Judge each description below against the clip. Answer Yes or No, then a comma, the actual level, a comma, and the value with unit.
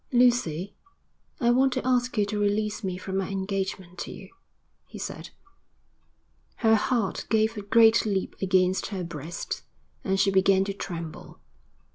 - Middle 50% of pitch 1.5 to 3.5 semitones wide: Yes, average, 2.7 semitones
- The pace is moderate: Yes, average, 150 wpm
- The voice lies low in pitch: No, high, 200 Hz